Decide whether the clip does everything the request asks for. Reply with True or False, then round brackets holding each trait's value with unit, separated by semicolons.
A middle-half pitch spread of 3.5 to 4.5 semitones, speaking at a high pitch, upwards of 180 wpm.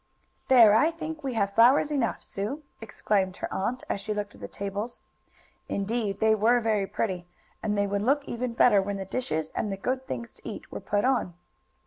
True (3.8 semitones; 220 Hz; 200 wpm)